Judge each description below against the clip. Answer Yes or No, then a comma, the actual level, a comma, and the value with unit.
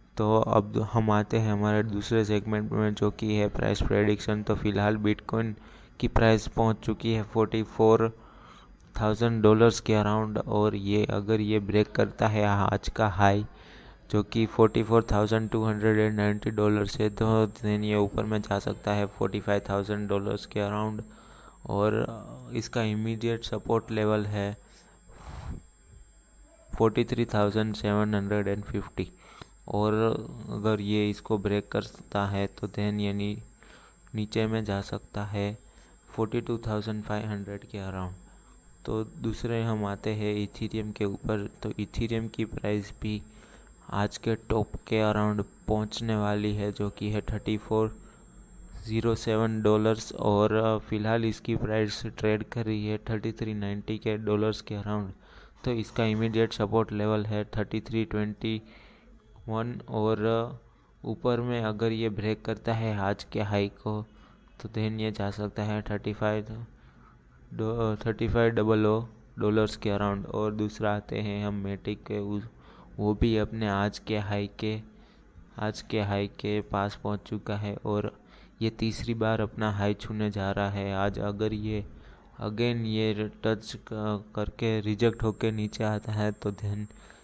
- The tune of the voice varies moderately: No, narrow, 1.3 semitones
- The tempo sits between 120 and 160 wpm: Yes, average, 145 wpm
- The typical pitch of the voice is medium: No, low, 105 Hz